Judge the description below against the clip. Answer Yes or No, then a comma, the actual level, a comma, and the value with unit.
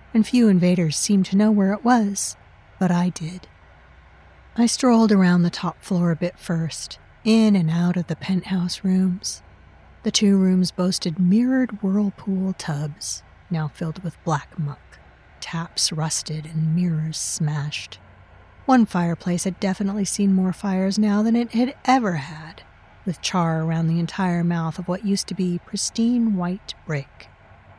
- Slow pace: No, average, 155 wpm